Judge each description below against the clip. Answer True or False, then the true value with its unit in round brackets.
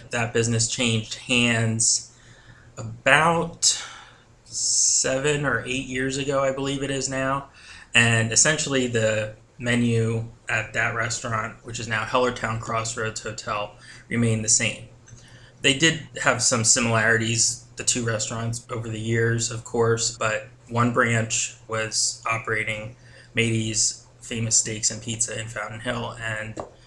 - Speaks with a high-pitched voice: False (115 Hz)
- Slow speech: True (130 wpm)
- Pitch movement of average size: False (1.8 semitones)